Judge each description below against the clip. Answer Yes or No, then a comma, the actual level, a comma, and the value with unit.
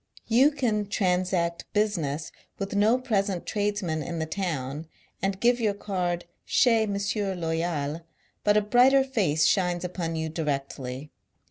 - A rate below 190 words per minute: Yes, average, 140 wpm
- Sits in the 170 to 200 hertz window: Yes, medium, 185 Hz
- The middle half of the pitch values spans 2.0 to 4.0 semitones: No, average, 4.5 semitones